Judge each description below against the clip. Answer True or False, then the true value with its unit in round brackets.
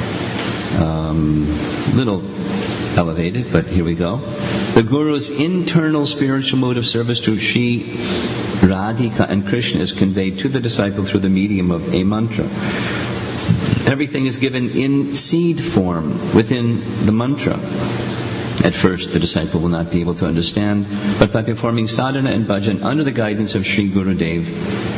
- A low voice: True (110 Hz)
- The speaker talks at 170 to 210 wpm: False (150 wpm)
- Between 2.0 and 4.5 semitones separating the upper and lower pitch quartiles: False (5.2 semitones)